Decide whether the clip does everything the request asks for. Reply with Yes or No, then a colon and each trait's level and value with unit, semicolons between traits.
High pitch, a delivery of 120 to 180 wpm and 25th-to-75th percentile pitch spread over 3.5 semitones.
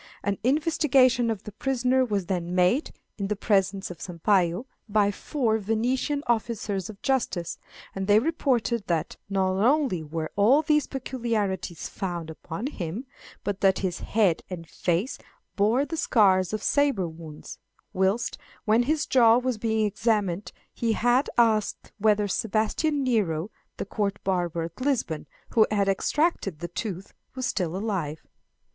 Yes: high, 210 Hz; average, 145 wpm; average, 4.5 semitones